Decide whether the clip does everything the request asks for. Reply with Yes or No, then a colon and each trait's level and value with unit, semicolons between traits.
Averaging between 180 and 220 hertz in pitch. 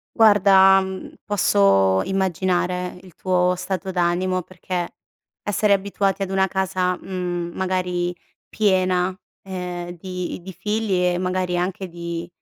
Yes: medium, 185 Hz